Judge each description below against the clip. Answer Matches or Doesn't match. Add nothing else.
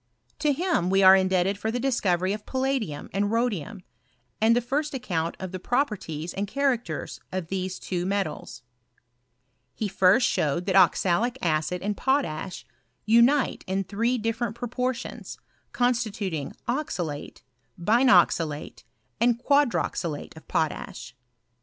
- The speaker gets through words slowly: Matches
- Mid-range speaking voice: Doesn't match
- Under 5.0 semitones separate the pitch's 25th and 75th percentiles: Doesn't match